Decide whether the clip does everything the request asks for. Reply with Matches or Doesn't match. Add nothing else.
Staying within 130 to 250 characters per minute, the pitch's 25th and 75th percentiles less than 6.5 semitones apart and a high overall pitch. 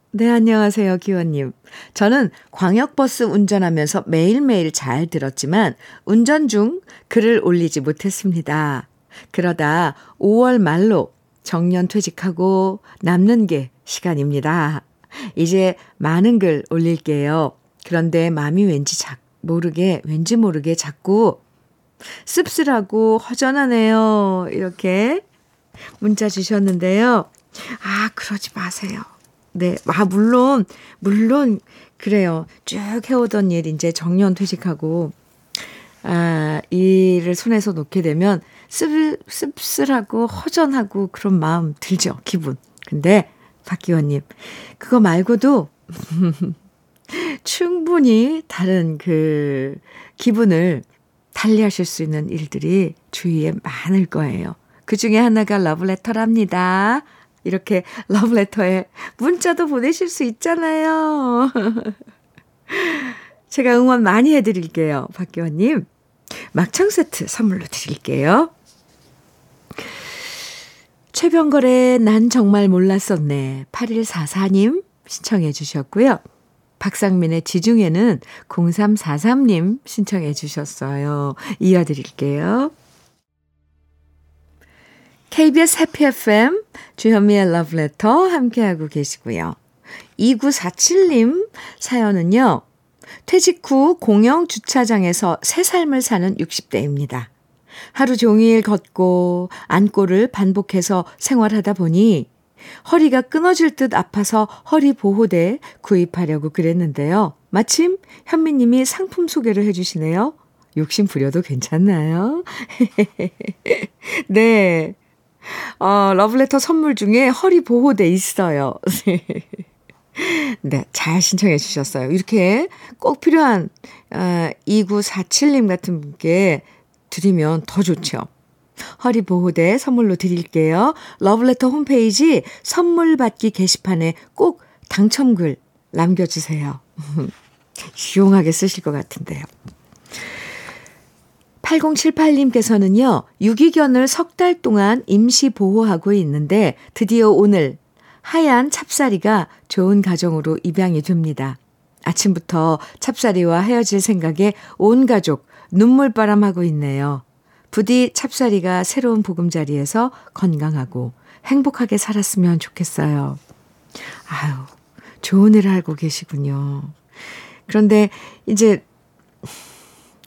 Matches